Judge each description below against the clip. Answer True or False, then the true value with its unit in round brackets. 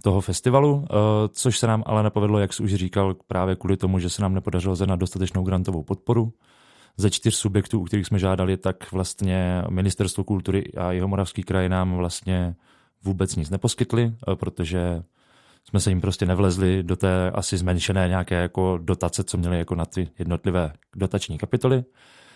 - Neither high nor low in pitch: False (95 Hz)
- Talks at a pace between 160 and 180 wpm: True (170 wpm)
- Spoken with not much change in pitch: True (2.3 semitones)